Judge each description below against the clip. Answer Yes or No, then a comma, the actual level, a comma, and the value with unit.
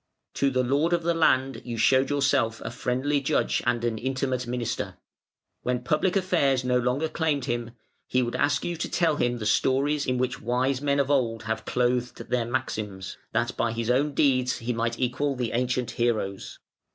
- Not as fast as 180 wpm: No, average, 190 wpm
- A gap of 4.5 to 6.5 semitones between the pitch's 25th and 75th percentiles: No, average, 2.7 semitones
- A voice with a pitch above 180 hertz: No, low, 125 Hz